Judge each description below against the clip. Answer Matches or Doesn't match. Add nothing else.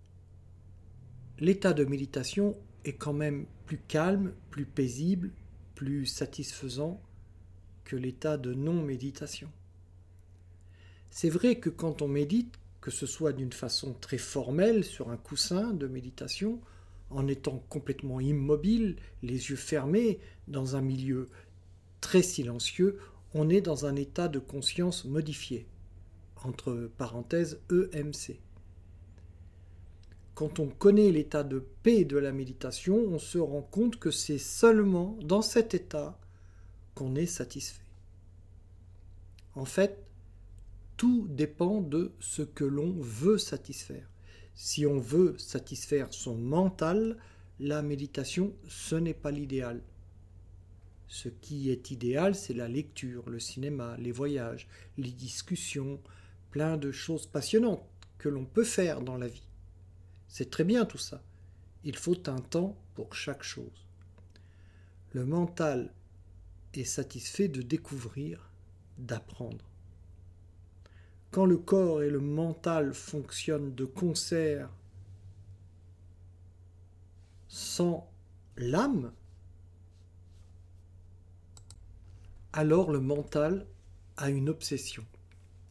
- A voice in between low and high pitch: Doesn't match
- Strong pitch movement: Matches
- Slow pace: Matches